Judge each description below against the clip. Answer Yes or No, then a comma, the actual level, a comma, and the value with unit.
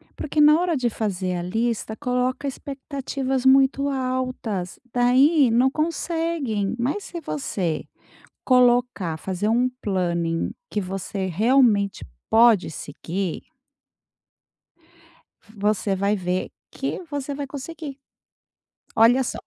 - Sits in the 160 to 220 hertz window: No, high, 245 Hz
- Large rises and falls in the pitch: Yes, wide, 5.8 semitones